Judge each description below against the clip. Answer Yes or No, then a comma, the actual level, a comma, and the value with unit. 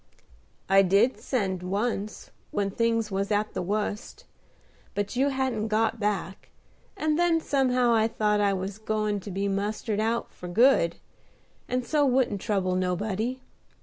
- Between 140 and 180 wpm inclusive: Yes, average, 150 wpm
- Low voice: No, high, 215 Hz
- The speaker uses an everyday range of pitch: Yes, average, 3.5 semitones